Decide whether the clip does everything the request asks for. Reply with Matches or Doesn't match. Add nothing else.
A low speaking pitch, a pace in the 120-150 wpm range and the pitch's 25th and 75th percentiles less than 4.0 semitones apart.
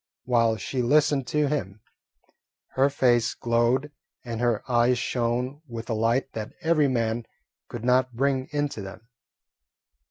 Matches